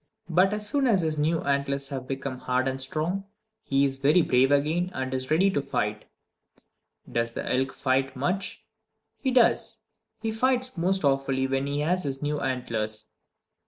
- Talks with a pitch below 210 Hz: Yes, medium, 140 Hz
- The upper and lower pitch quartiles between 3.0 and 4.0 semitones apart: No, average, 5.2 semitones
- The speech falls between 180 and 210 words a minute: No, average, 170 wpm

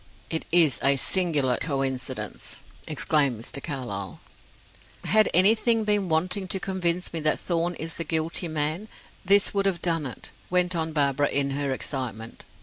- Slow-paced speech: No, average, 150 wpm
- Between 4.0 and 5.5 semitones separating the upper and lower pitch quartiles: Yes, average, 4.7 semitones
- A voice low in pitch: No, medium, 160 Hz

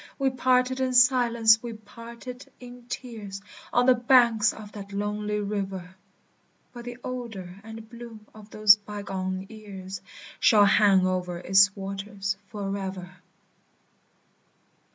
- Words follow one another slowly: Yes, slow, 120 wpm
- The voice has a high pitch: Yes, high, 210 Hz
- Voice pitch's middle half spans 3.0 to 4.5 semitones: Yes, average, 3.4 semitones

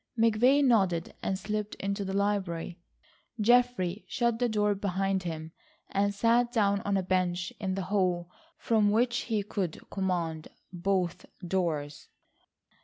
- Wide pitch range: No, average, 3.1 semitones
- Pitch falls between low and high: No, high, 195 Hz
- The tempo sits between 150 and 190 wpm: No, slow, 135 wpm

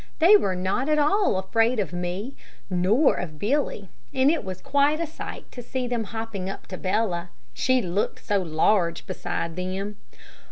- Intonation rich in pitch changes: Yes, wide, 6.0 semitones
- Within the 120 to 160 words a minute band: No, average, 170 wpm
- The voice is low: No, high, 205 Hz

